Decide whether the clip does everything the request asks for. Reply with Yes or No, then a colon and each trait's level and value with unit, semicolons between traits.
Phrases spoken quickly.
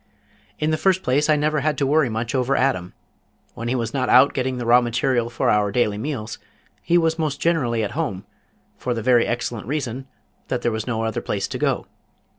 Yes: fast, 215 wpm